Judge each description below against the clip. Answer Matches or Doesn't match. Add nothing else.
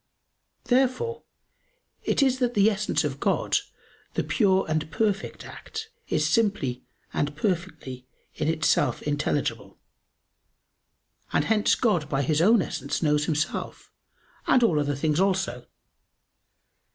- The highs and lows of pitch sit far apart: Matches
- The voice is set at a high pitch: Doesn't match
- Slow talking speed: Matches